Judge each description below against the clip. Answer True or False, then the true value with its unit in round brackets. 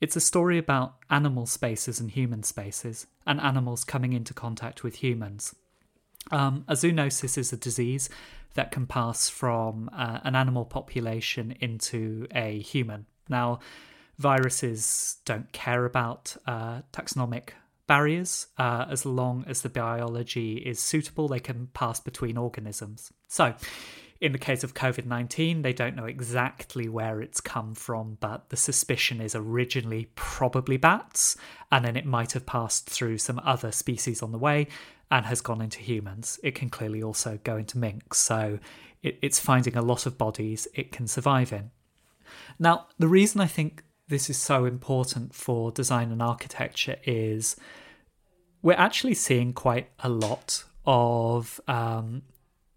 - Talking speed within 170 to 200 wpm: False (150 wpm)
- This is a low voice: True (125 Hz)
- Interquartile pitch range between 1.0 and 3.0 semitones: True (2.7 semitones)